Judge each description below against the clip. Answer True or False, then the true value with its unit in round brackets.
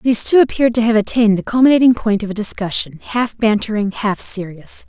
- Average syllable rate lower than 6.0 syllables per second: False (6.1 syllables/s)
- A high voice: True (220 Hz)